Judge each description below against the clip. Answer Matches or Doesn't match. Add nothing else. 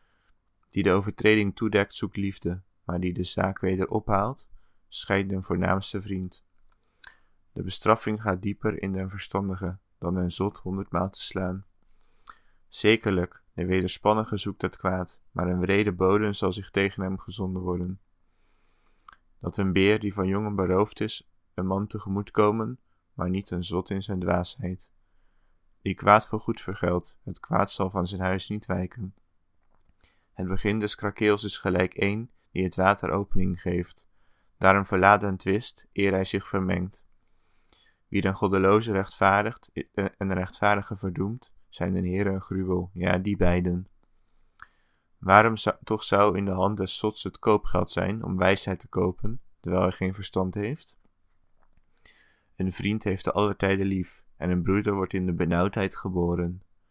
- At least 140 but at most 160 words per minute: Matches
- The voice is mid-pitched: Doesn't match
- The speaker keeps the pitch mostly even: Matches